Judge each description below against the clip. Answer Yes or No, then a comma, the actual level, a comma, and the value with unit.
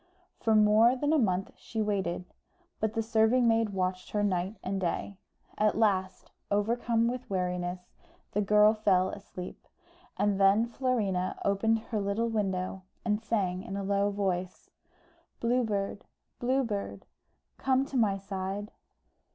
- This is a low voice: No, high, 205 Hz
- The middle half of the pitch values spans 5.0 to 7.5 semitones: No, average, 2.9 semitones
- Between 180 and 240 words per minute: No, average, 145 wpm